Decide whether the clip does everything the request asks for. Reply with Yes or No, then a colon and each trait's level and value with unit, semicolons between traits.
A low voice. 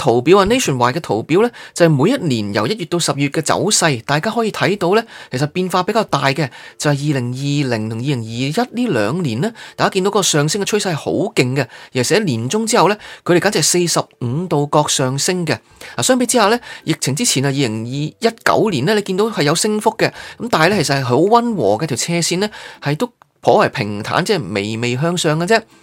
No: medium, 160 Hz